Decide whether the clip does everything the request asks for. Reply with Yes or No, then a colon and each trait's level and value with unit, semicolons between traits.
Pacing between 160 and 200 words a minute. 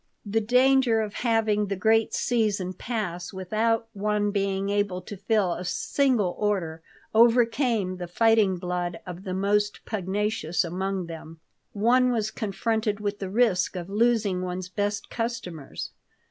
No: average, 140 wpm